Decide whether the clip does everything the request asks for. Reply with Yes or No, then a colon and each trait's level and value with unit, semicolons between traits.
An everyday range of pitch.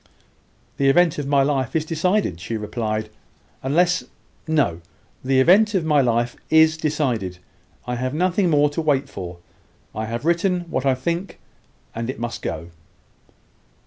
No: wide, 5.7 semitones